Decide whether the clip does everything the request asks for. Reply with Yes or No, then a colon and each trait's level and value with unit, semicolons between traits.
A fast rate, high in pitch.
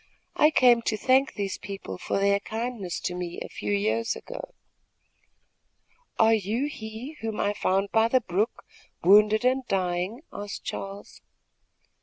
No: average, 145 wpm; high, 215 Hz